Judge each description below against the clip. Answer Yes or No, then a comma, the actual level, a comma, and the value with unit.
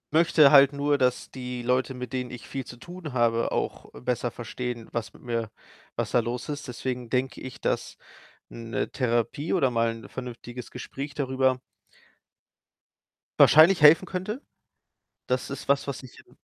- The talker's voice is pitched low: Yes, low, 125 Hz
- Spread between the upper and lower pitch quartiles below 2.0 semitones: No, average, 2.7 semitones